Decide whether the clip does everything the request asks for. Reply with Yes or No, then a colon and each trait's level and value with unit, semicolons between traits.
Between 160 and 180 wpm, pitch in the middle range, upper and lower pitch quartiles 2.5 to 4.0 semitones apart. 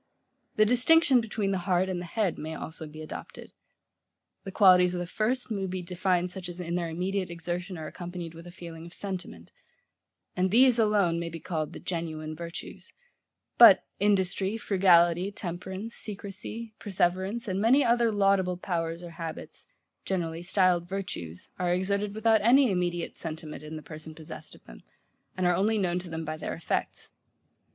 Yes: average, 170 wpm; medium, 180 Hz; average, 3.0 semitones